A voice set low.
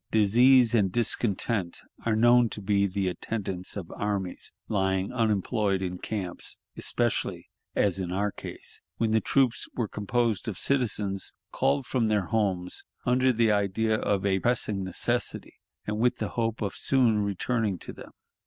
Yes: low, 105 Hz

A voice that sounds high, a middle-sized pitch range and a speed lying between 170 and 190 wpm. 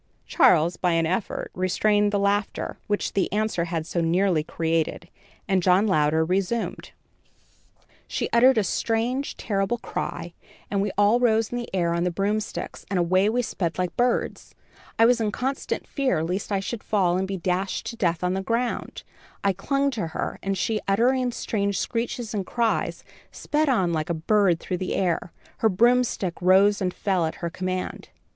Yes: high, 195 Hz; average, 4.0 semitones; average, 180 wpm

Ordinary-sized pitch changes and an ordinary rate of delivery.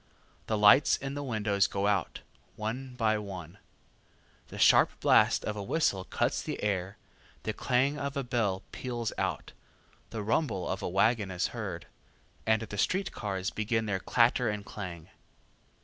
Yes: average, 3.8 semitones; average, 160 wpm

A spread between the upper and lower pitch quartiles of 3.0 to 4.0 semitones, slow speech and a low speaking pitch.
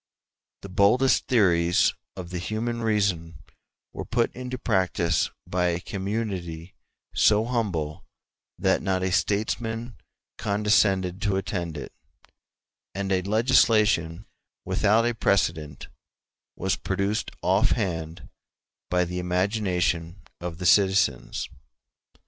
Yes: average, 3.5 semitones; slow, 110 wpm; very low, 95 Hz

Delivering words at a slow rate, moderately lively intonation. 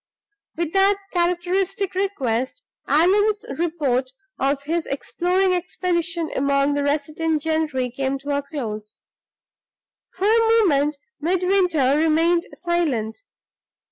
Yes: slow, 105 wpm; average, 4.4 semitones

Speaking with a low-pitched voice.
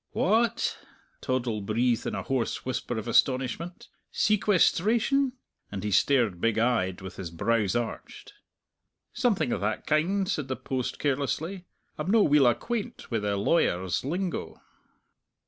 Yes: low, 130 Hz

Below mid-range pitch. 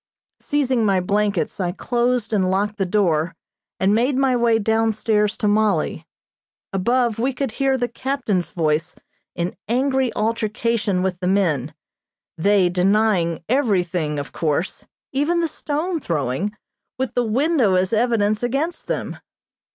No: high, 215 Hz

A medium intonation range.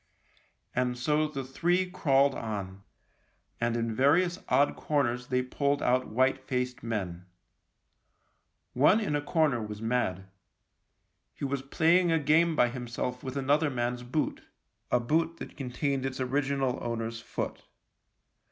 Yes: average, 3.4 semitones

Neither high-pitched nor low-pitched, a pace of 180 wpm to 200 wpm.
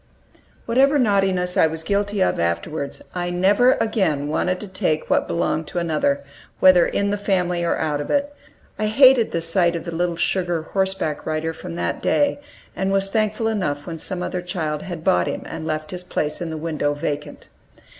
Yes: medium, 175 Hz; average, 190 wpm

